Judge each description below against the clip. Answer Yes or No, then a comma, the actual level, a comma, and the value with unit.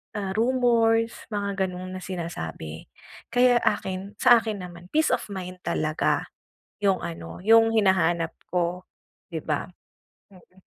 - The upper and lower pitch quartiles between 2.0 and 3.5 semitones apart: No, average, 4.4 semitones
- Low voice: No, high, 190 Hz